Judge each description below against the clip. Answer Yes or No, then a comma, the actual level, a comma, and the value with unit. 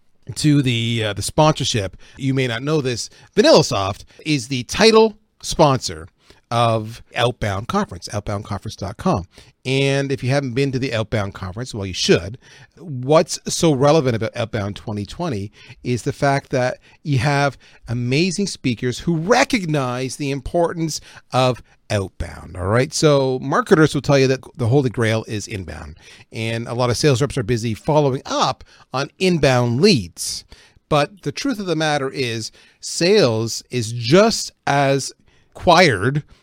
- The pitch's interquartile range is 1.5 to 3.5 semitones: No, average, 4.6 semitones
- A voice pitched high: No, low, 130 Hz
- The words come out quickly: No, average, 150 wpm